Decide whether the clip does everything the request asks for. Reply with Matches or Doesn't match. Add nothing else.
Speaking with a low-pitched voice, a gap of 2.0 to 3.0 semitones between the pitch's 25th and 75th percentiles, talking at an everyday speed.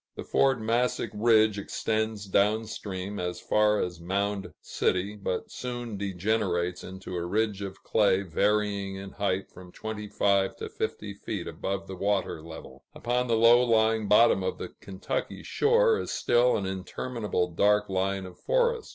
Matches